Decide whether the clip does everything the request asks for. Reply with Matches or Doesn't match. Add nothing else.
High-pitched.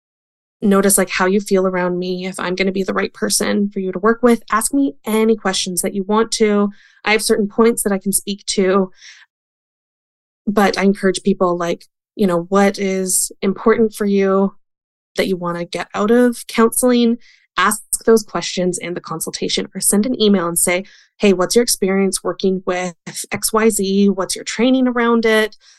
Matches